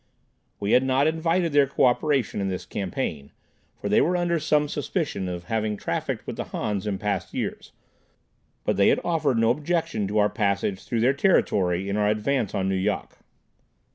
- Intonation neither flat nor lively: No, wide, 6.7 semitones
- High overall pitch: No, low, 110 Hz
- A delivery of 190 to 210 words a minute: No, average, 180 wpm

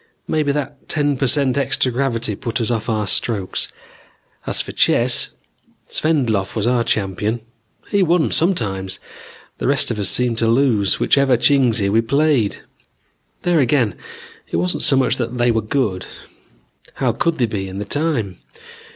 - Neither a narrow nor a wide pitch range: Yes, average, 4.7 semitones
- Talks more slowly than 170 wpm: Yes, average, 160 wpm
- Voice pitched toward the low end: Yes, low, 120 Hz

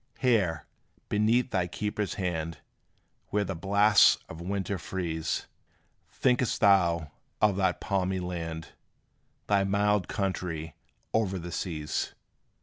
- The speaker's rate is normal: No, slow, 110 wpm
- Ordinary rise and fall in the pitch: Yes, average, 3.4 semitones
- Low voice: Yes, very low, 95 Hz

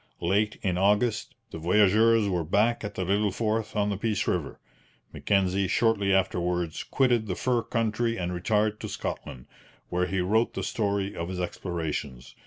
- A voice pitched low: Yes, low, 100 Hz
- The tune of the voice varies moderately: Yes, average, 3.3 semitones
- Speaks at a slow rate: No, average, 165 wpm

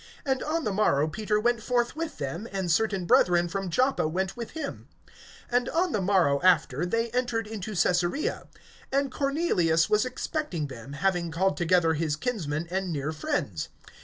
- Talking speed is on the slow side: No, average, 165 wpm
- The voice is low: No, high, 190 Hz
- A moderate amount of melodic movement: No, wide, 6.7 semitones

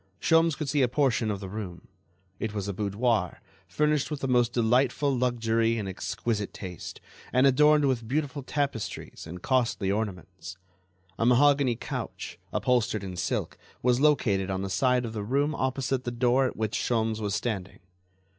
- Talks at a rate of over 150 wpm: Yes, average, 165 wpm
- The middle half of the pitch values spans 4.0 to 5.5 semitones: Yes, average, 4.5 semitones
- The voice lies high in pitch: No, low, 120 Hz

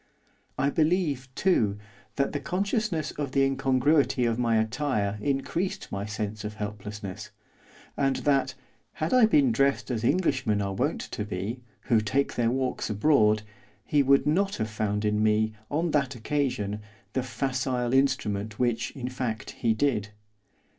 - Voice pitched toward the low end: Yes, low, 125 Hz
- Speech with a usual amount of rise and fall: Yes, average, 4.9 semitones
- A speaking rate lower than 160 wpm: Yes, average, 150 wpm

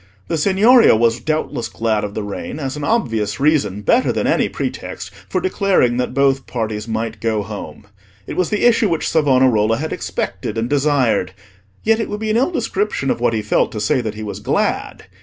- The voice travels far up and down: Yes, wide, 8.7 semitones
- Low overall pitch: Yes, low, 130 Hz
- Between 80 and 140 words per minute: No, average, 200 wpm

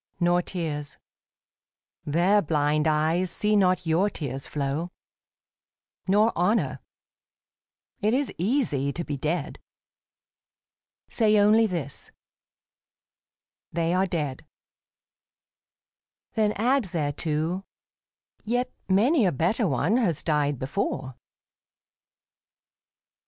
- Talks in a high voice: No, medium, 175 Hz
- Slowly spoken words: Yes, slow, 95 wpm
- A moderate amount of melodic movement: No, wide, 5.8 semitones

